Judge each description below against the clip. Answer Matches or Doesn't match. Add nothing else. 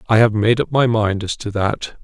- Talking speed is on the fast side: Matches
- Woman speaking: Doesn't match